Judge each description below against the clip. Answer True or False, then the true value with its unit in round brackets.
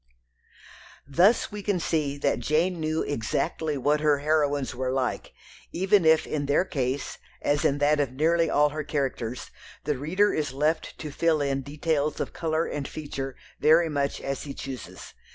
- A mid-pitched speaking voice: True (150 Hz)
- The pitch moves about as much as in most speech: False (2.3 semitones)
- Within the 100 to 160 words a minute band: False (170 wpm)